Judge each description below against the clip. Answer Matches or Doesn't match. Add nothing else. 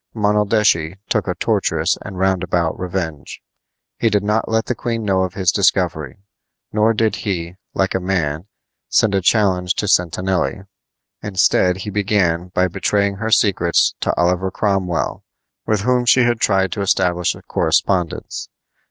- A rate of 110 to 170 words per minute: Matches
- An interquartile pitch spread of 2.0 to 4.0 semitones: Matches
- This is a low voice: Matches